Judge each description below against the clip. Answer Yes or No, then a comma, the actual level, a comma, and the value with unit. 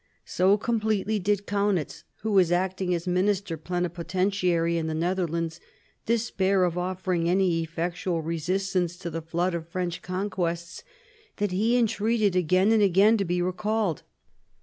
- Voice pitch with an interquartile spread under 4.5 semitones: Yes, average, 2.8 semitones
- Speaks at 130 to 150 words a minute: Yes, average, 140 wpm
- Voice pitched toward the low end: No, medium, 185 Hz